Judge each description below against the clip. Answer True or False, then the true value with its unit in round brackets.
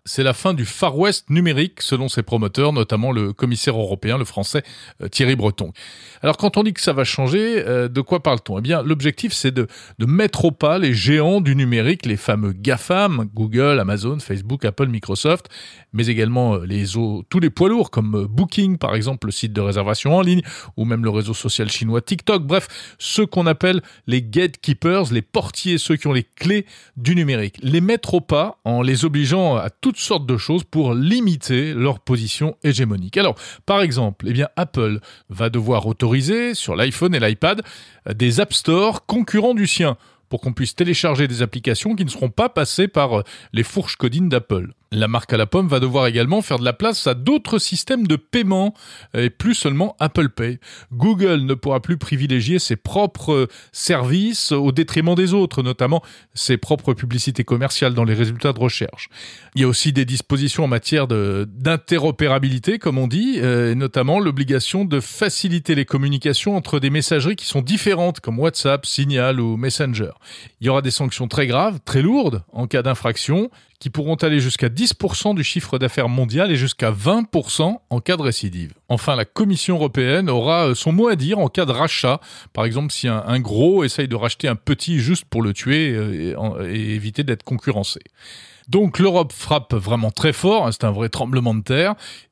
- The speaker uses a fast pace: False (190 wpm)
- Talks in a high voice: False (135 Hz)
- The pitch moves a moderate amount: False (6.3 semitones)